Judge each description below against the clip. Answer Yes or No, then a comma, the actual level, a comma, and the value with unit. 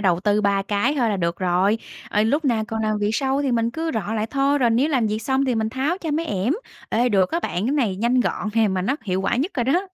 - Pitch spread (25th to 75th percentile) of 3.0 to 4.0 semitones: No, average, 4.8 semitones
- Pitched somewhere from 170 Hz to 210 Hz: No, high, 225 Hz